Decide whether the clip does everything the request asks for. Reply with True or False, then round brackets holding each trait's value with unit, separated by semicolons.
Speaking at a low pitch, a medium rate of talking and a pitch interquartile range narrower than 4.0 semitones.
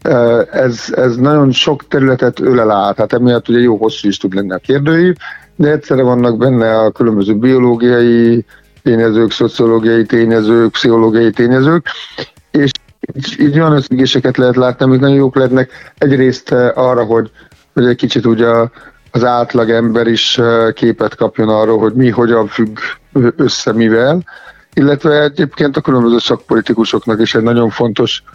True (120 Hz; 145 wpm; 2.4 semitones)